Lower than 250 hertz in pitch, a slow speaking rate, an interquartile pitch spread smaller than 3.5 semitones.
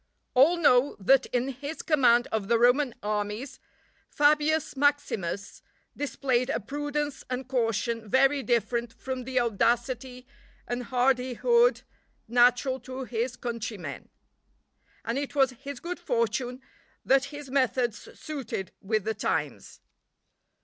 No: very high, 255 Hz; slow, 120 wpm; average, 2.8 semitones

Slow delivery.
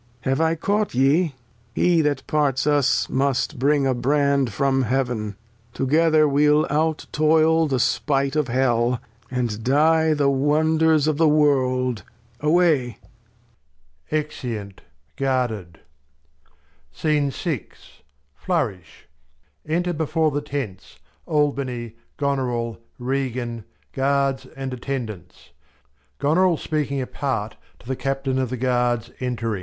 Yes: slow, 105 wpm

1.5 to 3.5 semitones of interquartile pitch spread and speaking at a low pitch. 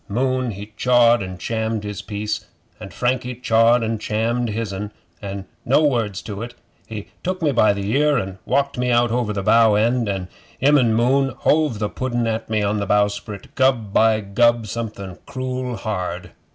Yes: average, 3.1 semitones; low, 115 Hz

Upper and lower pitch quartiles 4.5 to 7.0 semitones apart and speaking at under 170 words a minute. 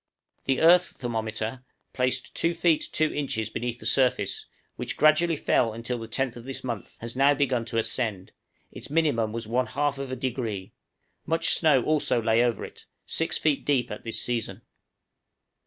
No: average, 4.1 semitones; average, 155 wpm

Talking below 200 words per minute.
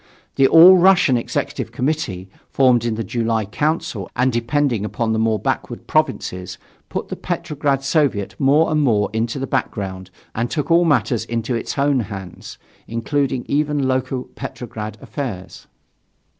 Yes: average, 145 wpm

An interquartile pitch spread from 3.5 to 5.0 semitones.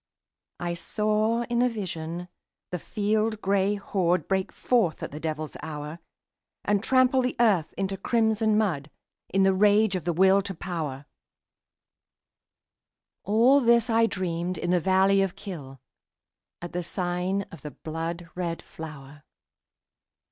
Yes: average, 4.2 semitones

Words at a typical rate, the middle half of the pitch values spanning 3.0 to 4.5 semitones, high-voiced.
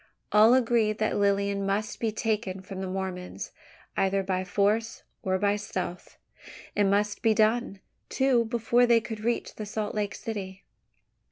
No: average, 155 wpm; narrow, 2.4 semitones; high, 210 Hz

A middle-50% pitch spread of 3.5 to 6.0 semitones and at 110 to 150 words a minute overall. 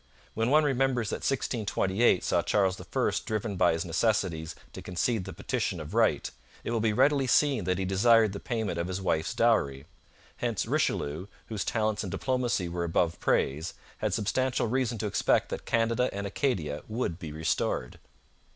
No: average, 5.2 semitones; average, 170 wpm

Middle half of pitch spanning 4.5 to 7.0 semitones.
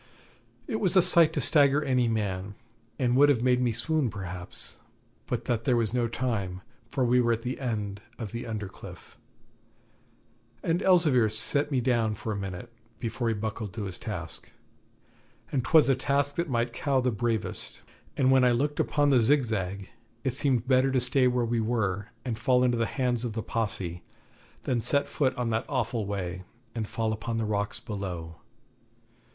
No: average, 3.5 semitones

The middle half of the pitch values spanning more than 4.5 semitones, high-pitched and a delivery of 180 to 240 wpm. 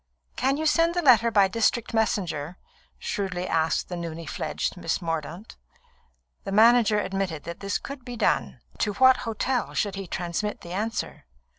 No: average, 5.2 semitones; high, 205 Hz; average, 160 wpm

